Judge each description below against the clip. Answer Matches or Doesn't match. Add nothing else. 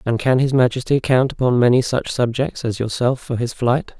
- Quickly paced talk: Matches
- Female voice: Doesn't match